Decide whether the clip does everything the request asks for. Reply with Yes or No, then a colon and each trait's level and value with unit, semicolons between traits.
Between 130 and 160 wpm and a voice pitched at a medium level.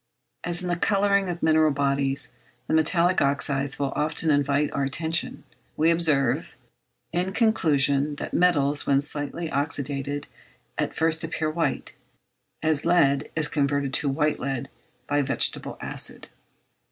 Yes: slow, 135 wpm; medium, 150 Hz